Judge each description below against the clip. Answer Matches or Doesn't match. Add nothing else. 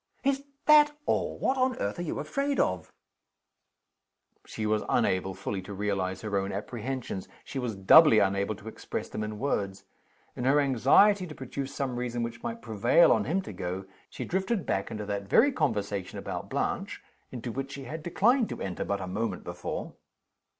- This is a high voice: Doesn't match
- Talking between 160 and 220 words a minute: Matches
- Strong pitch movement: Matches